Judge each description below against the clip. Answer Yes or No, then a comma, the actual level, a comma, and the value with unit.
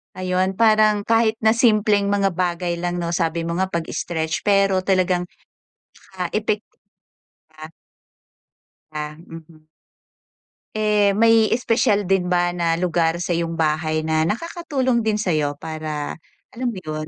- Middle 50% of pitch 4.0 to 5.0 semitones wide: Yes, average, 4.4 semitones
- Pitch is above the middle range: No, medium, 180 Hz